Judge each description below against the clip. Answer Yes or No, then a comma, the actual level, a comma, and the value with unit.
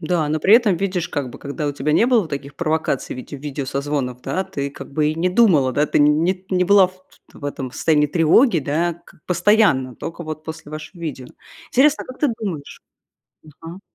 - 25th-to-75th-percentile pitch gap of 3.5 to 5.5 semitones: Yes, average, 4.2 semitones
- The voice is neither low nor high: Yes, medium, 155 Hz